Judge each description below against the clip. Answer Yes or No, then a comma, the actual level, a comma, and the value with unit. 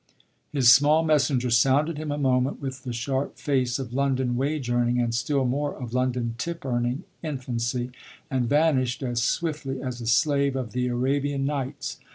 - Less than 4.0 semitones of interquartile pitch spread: Yes, narrow, 2.6 semitones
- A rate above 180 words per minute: No, average, 170 wpm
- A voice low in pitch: Yes, low, 130 Hz